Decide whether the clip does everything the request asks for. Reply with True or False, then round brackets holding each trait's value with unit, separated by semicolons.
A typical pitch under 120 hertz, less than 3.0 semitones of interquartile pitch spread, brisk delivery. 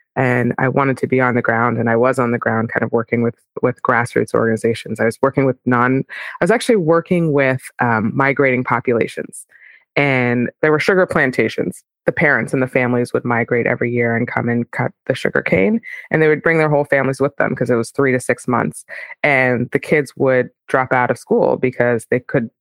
False (125 Hz; 2.6 semitones; 220 wpm)